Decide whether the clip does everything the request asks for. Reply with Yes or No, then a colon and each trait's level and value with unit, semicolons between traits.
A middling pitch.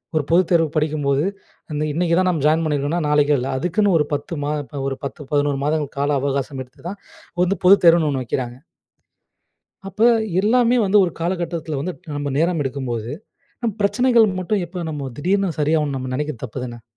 Yes: medium, 155 Hz